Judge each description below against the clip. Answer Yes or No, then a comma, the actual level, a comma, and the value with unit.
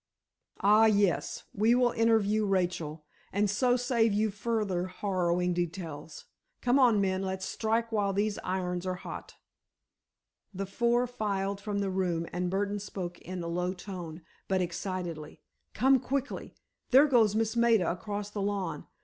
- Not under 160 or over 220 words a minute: No, average, 150 wpm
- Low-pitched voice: No, high, 200 Hz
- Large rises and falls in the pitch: No, average, 3.5 semitones